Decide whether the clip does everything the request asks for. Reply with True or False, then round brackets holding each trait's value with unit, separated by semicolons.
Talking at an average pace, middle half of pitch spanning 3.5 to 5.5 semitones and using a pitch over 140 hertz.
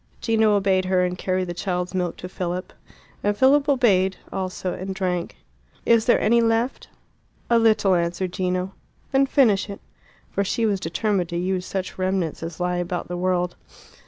False (170 wpm; 2.9 semitones; 185 Hz)